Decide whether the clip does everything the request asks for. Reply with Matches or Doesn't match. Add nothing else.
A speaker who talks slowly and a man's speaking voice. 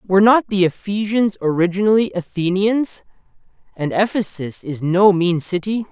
Matches